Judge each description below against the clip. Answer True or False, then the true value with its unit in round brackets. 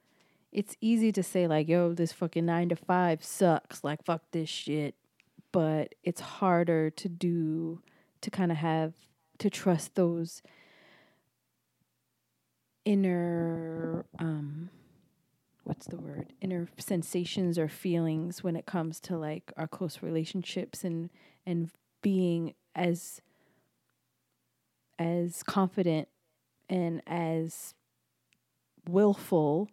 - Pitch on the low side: False (170 Hz)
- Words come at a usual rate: False (110 wpm)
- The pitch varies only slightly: True (2.0 semitones)